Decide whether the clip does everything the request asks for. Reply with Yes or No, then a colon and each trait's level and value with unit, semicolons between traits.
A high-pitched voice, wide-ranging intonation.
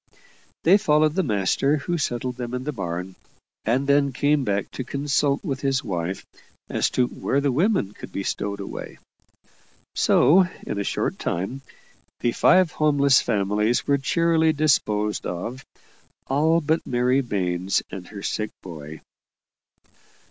No: low, 130 Hz; wide, 6.4 semitones